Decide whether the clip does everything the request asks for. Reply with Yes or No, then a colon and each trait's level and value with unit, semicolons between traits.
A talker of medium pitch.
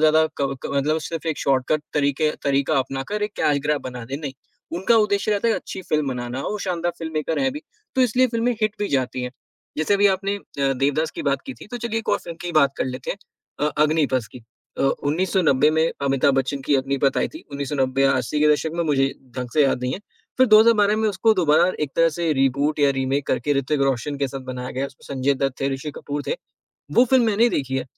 Yes: medium, 150 Hz